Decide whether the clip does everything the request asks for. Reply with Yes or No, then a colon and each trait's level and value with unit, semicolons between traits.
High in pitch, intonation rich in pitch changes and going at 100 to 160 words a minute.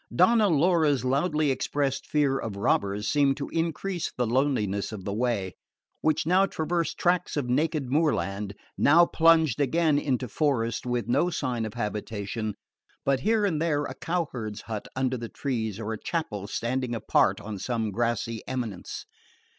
No: low, 130 Hz; wide, 5.9 semitones; average, 155 wpm